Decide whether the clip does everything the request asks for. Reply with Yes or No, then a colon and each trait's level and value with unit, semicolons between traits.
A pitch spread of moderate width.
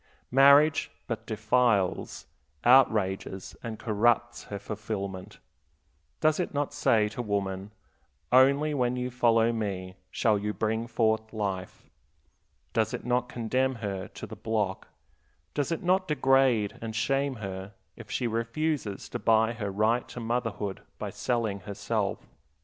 Yes: average, 3.6 semitones